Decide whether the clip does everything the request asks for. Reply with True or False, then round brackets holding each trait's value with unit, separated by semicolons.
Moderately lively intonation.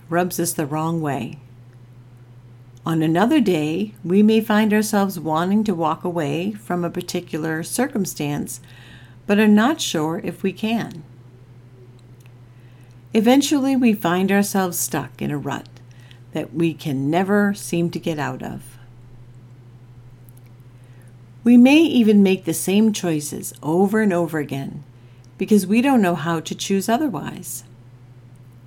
False (8.0 semitones)